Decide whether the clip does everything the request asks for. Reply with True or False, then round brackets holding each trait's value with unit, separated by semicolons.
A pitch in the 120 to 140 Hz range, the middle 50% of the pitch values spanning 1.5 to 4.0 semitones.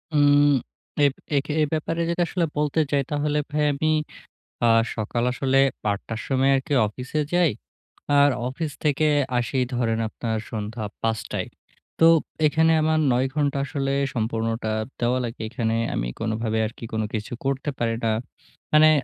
False (135 Hz; 4.7 semitones)